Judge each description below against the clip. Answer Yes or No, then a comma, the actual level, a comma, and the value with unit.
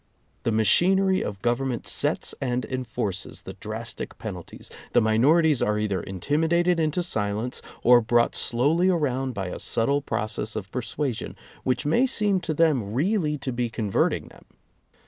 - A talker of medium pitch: No, low, 125 Hz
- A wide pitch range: Yes, wide, 6.4 semitones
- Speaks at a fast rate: No, average, 155 wpm